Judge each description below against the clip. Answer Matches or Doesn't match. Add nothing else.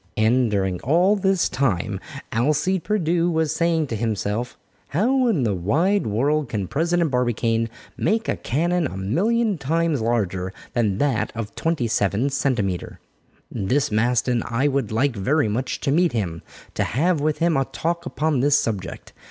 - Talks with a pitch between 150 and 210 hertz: Doesn't match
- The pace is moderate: Matches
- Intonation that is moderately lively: Doesn't match